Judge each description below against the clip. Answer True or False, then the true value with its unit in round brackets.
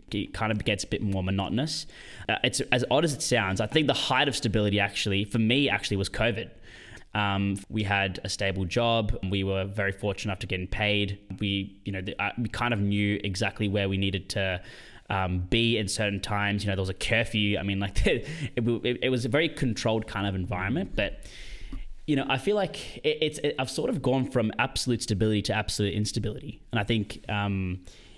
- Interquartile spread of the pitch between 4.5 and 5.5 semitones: False (3.4 semitones)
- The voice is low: True (105 Hz)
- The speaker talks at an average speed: False (220 wpm)